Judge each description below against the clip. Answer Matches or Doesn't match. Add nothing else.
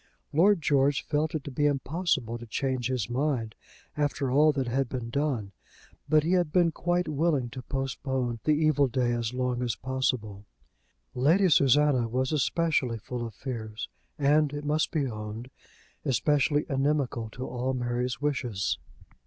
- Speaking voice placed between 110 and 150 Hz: Matches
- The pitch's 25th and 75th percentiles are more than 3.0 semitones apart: Matches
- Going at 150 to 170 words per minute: Matches